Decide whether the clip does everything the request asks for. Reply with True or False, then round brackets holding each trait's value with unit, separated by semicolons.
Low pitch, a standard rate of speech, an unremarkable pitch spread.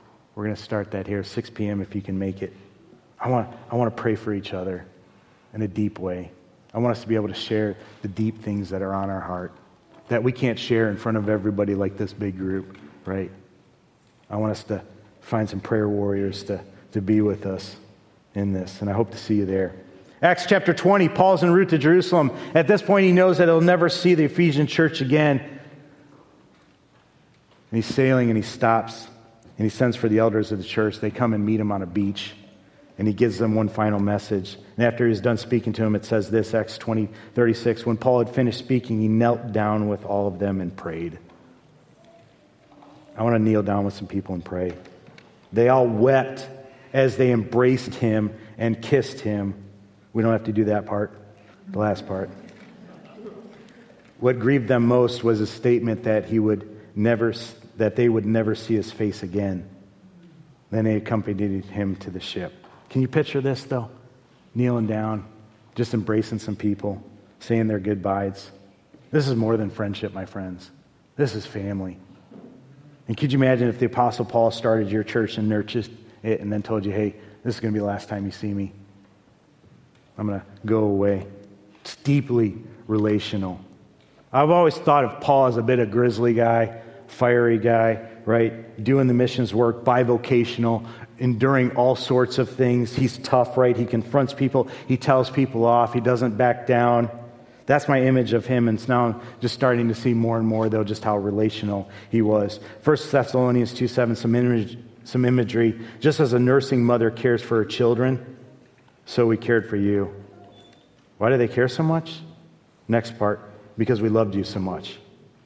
True (115 Hz; 190 wpm; 3.4 semitones)